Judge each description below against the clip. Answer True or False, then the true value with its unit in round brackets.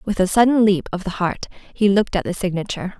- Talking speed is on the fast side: True (240 wpm)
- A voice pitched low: False (195 Hz)